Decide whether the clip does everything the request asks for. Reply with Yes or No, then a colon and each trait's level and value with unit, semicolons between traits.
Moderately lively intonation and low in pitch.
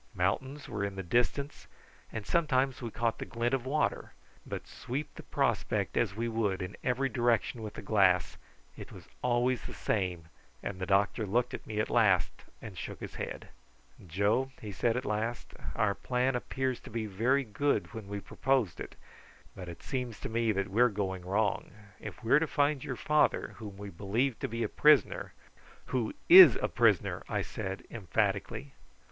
Yes: average, 4.2 semitones; low, 115 Hz